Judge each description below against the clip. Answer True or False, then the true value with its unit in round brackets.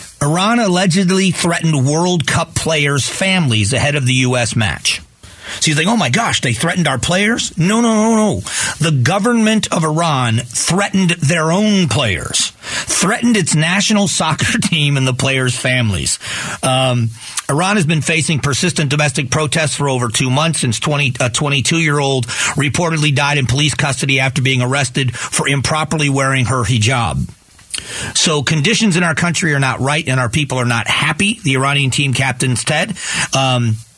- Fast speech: False (165 wpm)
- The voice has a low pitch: False (145 Hz)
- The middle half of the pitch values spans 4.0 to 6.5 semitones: True (4.7 semitones)